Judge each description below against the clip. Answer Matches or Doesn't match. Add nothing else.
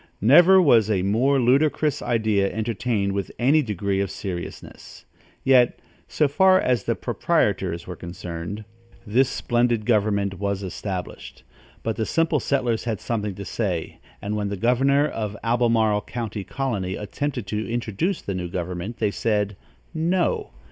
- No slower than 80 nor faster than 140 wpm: Doesn't match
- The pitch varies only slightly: Doesn't match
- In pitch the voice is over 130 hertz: Doesn't match